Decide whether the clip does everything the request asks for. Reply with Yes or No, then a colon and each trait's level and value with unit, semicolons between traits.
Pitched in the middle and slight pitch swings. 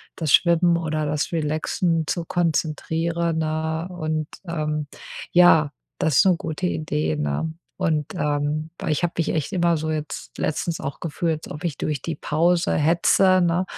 Yes: medium, 160 Hz; narrow, 1.9 semitones